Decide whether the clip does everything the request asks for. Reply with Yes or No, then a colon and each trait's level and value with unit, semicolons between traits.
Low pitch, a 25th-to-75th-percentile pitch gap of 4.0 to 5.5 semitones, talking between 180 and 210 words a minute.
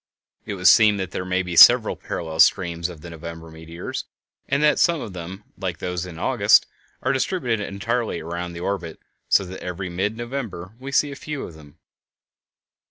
Yes: very low, 90 Hz; average, 4.3 semitones; average, 185 wpm